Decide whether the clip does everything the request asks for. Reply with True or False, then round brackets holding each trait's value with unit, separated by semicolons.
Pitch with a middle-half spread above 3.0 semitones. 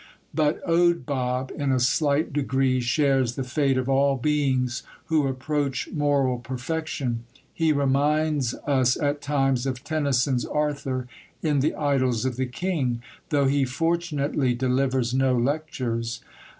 False (2.5 semitones)